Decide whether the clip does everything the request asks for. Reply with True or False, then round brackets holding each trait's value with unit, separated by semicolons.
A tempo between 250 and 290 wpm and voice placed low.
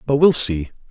False (200 wpm; 130 Hz)